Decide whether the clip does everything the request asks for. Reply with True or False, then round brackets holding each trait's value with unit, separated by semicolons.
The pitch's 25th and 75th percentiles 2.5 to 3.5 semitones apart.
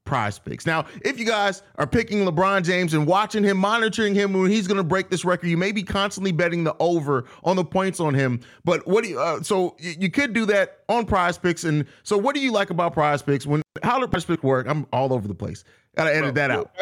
False (4.5 semitones)